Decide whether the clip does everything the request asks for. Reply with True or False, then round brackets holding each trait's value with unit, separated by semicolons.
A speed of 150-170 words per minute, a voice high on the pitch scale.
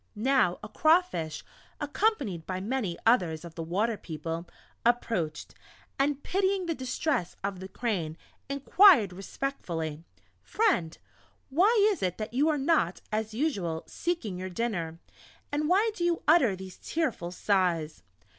False (135 wpm; 220 Hz)